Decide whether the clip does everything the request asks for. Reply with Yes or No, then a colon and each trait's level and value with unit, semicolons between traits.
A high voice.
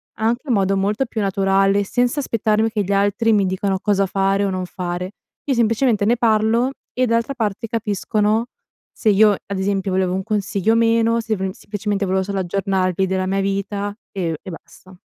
Yes: high, 200 Hz